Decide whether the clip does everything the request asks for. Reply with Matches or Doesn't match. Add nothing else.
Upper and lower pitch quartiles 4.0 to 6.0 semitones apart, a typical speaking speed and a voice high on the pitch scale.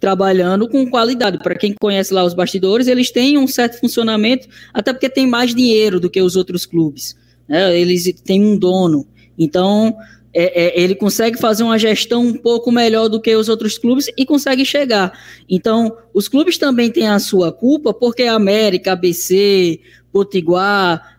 Matches